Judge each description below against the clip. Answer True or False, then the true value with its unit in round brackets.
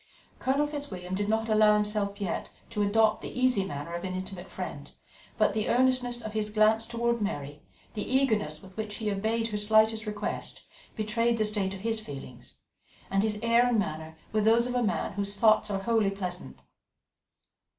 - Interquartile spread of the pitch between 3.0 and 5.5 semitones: False (2.6 semitones)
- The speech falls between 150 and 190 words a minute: True (180 wpm)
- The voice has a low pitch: False (215 Hz)